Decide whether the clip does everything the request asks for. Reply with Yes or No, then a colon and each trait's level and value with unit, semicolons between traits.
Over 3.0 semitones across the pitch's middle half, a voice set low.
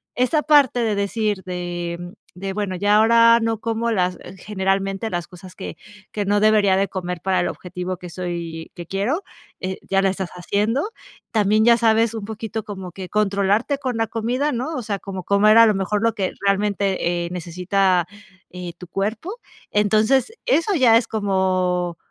No: average, 3.4 semitones; high, 200 Hz